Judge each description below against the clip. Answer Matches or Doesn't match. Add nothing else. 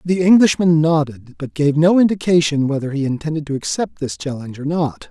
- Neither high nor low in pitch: Matches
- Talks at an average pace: Matches